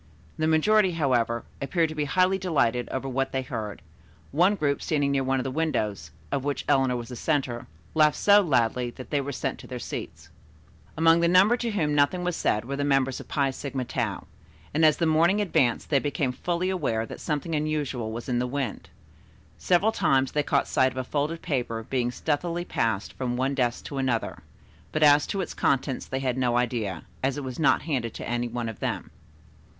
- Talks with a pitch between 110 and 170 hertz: Yes, medium, 140 Hz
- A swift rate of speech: Yes, fast, 210 wpm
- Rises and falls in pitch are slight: No, average, 4.2 semitones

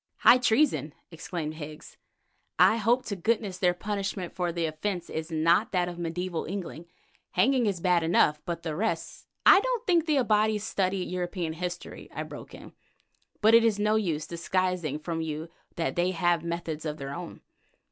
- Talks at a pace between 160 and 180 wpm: Yes, average, 170 wpm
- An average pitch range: Yes, average, 4.2 semitones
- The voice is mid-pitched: Yes, medium, 180 Hz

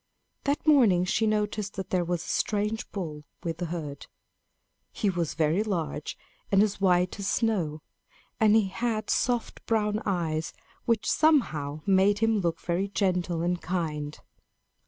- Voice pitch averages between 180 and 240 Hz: Yes, high, 190 Hz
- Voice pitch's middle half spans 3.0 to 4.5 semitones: Yes, average, 4.2 semitones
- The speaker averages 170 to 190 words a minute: No, average, 150 wpm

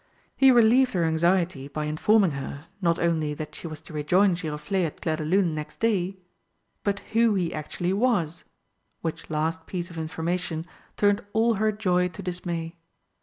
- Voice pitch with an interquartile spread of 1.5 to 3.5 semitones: No, average, 3.9 semitones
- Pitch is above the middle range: No, medium, 175 Hz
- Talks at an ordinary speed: Yes, average, 160 wpm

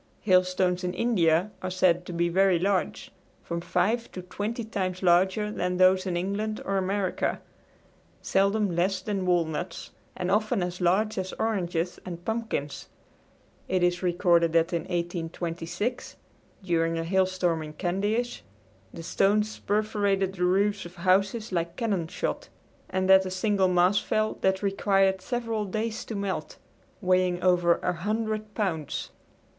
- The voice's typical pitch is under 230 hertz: Yes, medium, 185 Hz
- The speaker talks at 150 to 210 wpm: No, average, 140 wpm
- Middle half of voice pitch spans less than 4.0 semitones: Yes, average, 2.7 semitones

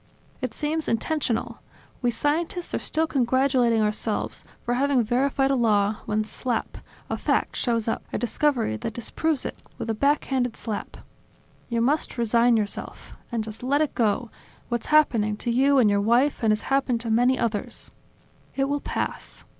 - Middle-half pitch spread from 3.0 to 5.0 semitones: Yes, average, 3.7 semitones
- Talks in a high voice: Yes, high, 240 Hz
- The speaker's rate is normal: Yes, average, 170 wpm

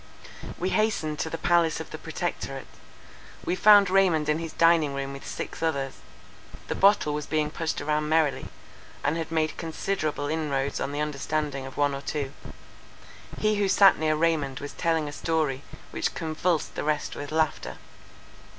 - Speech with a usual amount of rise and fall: No, narrow, 2.3 semitones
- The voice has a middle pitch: Yes, medium, 155 Hz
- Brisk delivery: No, average, 170 wpm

